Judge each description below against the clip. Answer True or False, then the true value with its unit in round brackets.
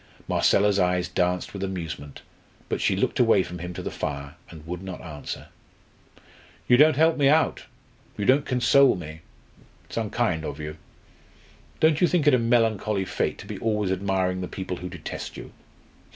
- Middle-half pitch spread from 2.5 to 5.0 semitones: False (5.5 semitones)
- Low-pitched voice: True (95 Hz)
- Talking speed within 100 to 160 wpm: False (175 wpm)